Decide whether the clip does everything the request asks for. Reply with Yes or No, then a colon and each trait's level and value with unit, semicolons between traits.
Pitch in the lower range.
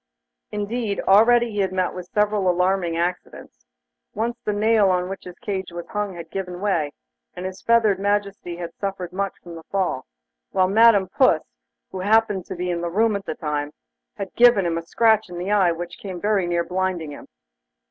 No: high, 190 Hz